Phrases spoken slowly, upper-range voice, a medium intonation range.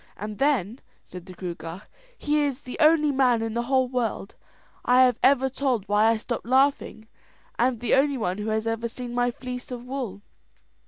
No: average, 190 wpm; high, 245 Hz; average, 3.4 semitones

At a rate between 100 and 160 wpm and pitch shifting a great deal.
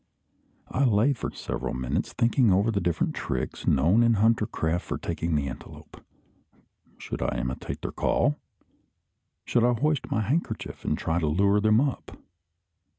Yes: average, 155 wpm; wide, 6.2 semitones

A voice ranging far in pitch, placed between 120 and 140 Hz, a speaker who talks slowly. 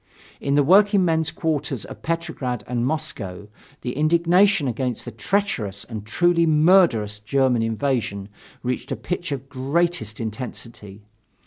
Yes: wide, 6.7 semitones; low, 135 Hz; slow, 125 wpm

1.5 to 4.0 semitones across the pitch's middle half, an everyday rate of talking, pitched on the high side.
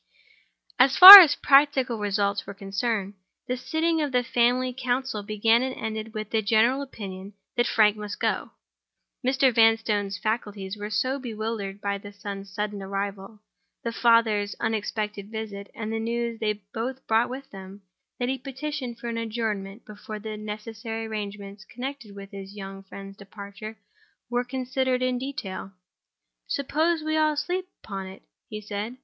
Yes: average, 3.7 semitones; average, 155 wpm; high, 220 Hz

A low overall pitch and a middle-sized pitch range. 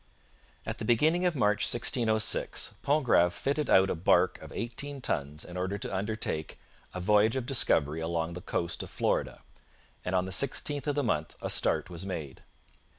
No: low, 100 Hz; wide, 6.9 semitones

